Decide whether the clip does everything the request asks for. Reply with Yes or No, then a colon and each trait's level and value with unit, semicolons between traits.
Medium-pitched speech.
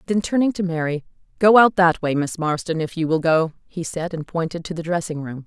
Yes: medium, 170 Hz